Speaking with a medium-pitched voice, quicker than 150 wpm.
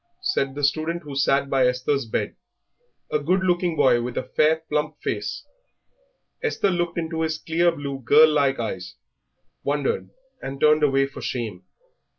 Yes: medium, 150 Hz; average, 160 wpm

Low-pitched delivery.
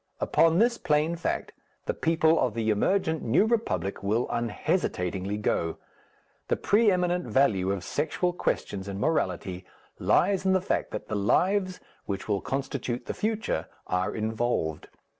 Yes: low, 125 Hz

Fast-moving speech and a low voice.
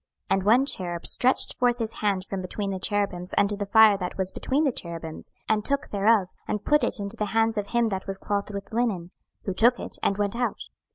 No: fast, 230 wpm; high, 205 Hz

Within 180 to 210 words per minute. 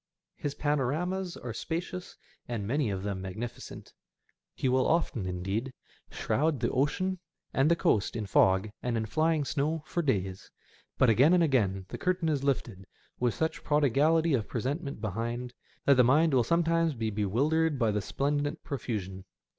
No: average, 160 wpm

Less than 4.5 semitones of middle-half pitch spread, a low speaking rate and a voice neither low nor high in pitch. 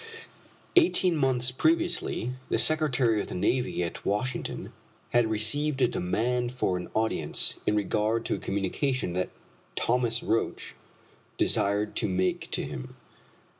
No: average, 4.0 semitones; slow, 130 wpm; low, 115 Hz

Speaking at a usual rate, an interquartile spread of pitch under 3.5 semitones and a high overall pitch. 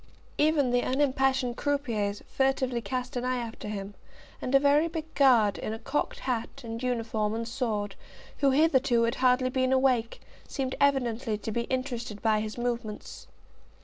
Yes: average, 160 wpm; average, 2.9 semitones; very high, 250 Hz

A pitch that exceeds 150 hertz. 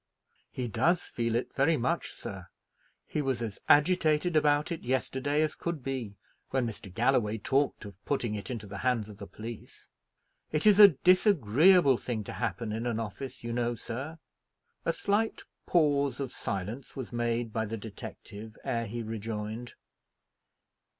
No: low, 120 Hz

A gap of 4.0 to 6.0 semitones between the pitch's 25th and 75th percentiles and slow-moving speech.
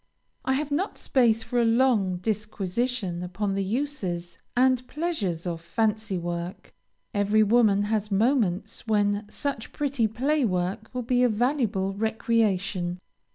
Yes: average, 4.3 semitones; slow, 130 wpm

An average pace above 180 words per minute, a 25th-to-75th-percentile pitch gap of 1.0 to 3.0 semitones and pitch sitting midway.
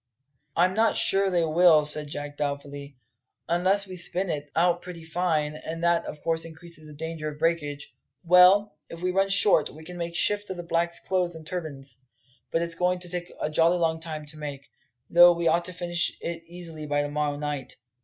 Yes: fast, 205 wpm; average, 2.7 semitones; medium, 165 Hz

